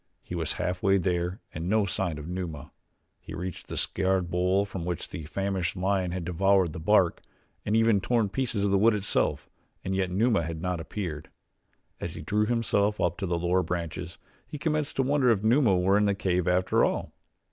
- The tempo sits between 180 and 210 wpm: Yes, average, 200 wpm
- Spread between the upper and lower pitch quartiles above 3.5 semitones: No, average, 2.8 semitones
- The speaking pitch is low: Yes, very low, 95 Hz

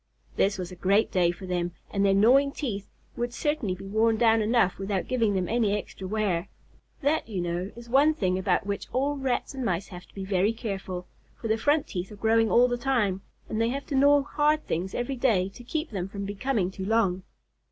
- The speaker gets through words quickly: Yes, fast, 220 wpm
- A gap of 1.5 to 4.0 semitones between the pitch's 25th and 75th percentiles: No, average, 4.4 semitones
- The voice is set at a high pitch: Yes, high, 215 Hz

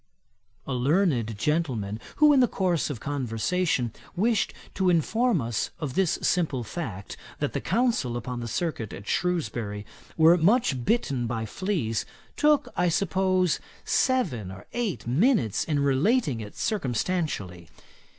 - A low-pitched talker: No, medium, 155 Hz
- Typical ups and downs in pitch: No, wide, 8.2 semitones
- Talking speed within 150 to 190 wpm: No, slow, 135 wpm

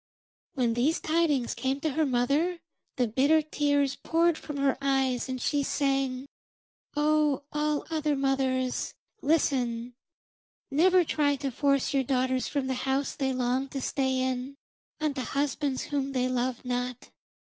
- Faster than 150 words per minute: No, average, 145 wpm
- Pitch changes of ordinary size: No, narrow, 2.3 semitones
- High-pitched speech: Yes, very high, 275 Hz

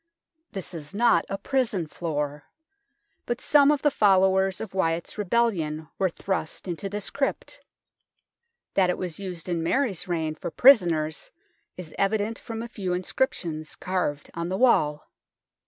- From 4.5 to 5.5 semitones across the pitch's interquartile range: Yes, average, 4.9 semitones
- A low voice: No, medium, 185 Hz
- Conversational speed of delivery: Yes, average, 145 wpm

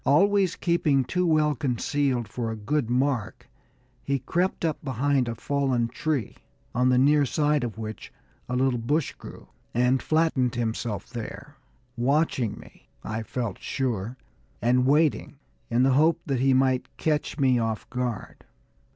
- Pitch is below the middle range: Yes, low, 130 Hz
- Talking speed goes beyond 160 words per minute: No, average, 150 wpm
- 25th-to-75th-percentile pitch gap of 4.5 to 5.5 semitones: No, average, 3.6 semitones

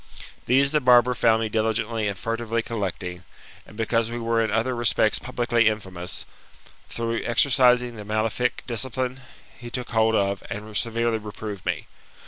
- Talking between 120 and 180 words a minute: Yes, average, 150 wpm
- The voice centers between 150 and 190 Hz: No, low, 115 Hz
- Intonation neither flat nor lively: No, narrow, 2.0 semitones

